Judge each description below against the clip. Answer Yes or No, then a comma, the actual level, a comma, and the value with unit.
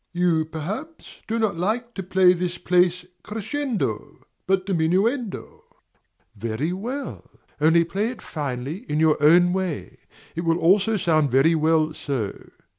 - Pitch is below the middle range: No, medium, 175 Hz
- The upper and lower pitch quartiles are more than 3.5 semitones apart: Yes, average, 4.2 semitones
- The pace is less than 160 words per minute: Yes, slow, 135 wpm